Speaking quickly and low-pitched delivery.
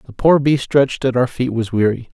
Yes: fast, 245 wpm; low, 125 Hz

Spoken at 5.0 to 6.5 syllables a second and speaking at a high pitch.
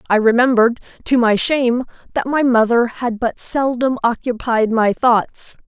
No: 4.6 syllables/s; high, 240 Hz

